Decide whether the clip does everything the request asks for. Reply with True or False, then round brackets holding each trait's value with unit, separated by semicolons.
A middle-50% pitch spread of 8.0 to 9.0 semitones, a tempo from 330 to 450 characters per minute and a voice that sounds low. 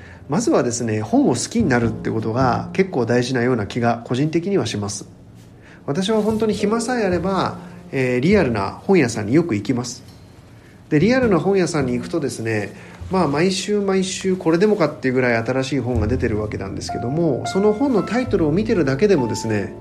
False (8.6 semitones; 320 characters per minute; 130 Hz)